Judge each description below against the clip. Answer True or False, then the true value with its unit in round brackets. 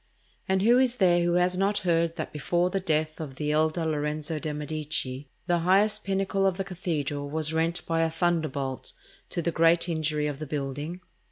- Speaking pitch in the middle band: True (165 Hz)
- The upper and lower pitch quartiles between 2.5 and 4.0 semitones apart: True (3.1 semitones)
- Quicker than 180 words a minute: True (190 wpm)